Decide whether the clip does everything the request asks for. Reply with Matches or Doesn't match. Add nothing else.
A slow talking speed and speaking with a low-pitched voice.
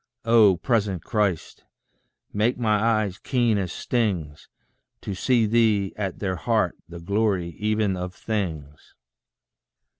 Matches